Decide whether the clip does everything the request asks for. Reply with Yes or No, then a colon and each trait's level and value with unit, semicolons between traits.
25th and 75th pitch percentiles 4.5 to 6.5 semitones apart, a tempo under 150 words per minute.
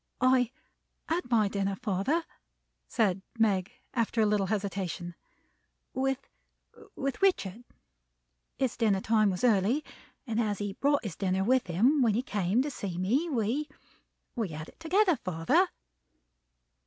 Yes: average, 5.1 semitones; average, 140 wpm